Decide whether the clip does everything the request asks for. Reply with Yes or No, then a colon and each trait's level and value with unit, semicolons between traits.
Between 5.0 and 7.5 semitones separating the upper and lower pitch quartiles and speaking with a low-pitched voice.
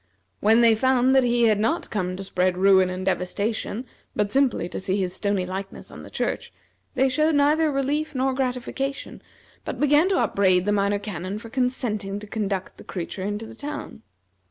No: wide, 5.4 semitones; high, 215 Hz